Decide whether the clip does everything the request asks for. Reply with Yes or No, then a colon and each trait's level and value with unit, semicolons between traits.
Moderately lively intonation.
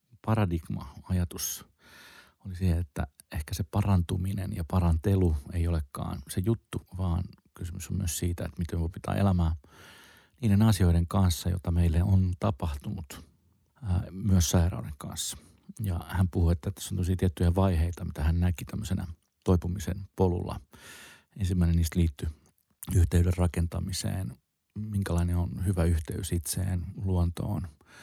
No: narrow, 2.1 semitones